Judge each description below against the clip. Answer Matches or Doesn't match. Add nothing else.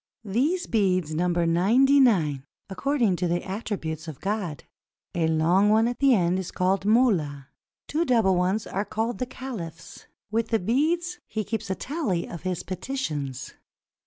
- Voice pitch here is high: Matches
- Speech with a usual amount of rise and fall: Doesn't match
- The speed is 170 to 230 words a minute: Doesn't match